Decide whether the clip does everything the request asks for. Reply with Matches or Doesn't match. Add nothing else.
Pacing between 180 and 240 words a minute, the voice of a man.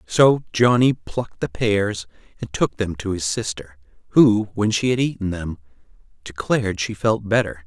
Doesn't match